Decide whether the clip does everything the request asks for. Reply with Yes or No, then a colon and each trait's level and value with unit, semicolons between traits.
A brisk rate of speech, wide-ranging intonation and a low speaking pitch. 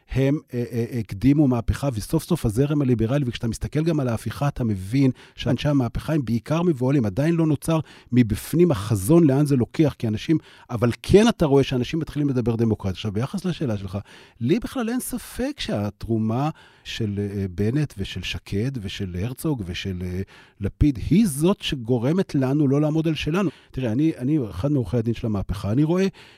Yes: fast, 175 wpm; wide, 5.7 semitones; low, 130 Hz